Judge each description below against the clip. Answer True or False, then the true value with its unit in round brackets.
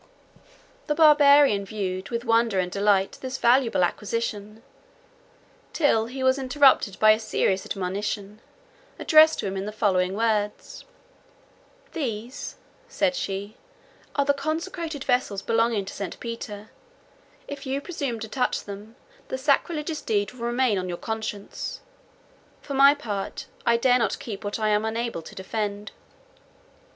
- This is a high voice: True (225 Hz)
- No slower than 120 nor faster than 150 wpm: True (140 wpm)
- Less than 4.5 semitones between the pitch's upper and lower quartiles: False (4.8 semitones)